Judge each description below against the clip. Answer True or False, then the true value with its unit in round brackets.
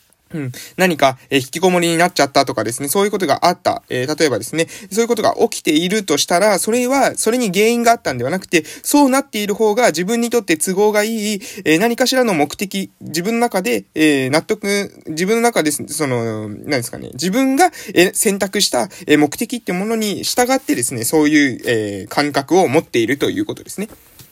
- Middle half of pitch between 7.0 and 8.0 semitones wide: True (7.5 semitones)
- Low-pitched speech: False (190 Hz)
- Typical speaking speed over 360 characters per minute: True (385 characters per minute)